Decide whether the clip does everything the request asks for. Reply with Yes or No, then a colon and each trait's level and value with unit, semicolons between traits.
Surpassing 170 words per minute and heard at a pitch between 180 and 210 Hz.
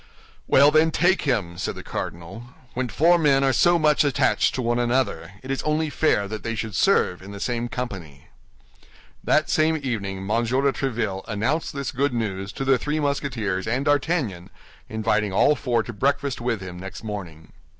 No: average, 180 wpm; low, 120 Hz